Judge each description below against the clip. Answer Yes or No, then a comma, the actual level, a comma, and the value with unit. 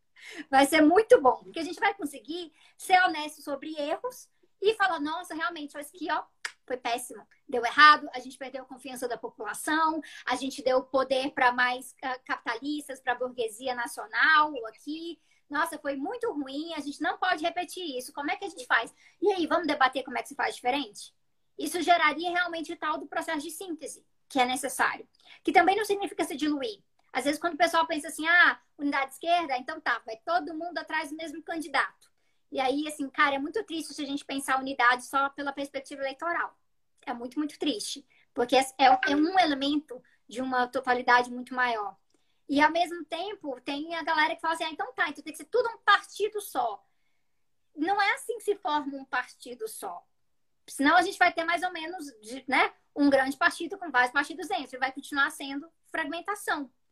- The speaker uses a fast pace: Yes, fast, 200 wpm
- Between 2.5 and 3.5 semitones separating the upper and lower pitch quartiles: No, average, 4.6 semitones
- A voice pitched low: No, very high, 300 Hz